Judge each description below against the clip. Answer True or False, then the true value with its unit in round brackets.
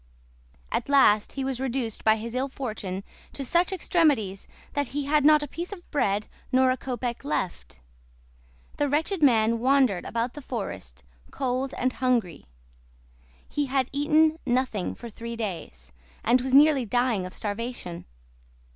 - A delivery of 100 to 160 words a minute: True (150 wpm)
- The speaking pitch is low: False (255 Hz)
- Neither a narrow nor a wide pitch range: True (4.4 semitones)